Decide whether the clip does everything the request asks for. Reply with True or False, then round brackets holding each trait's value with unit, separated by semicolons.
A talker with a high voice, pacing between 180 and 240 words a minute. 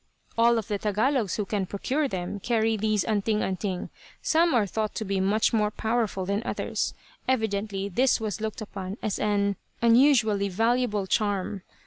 False (215 Hz; 160 wpm)